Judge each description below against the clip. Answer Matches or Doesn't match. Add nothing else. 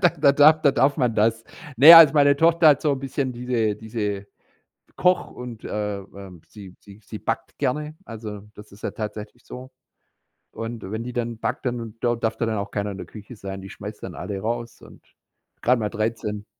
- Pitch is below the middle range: Matches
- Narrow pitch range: Doesn't match